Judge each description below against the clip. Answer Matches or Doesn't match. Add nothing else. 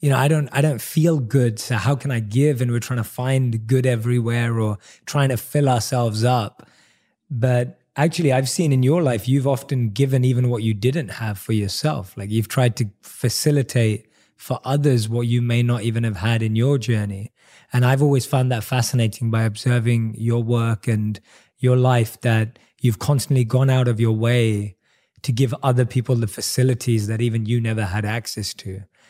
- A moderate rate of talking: Matches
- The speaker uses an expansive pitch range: Doesn't match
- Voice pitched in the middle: Doesn't match